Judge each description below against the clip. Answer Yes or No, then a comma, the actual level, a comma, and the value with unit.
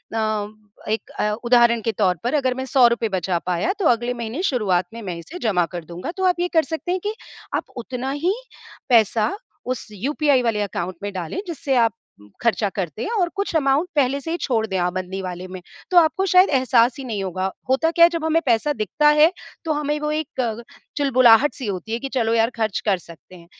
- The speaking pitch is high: Yes, high, 235 Hz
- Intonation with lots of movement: Yes, wide, 6.3 semitones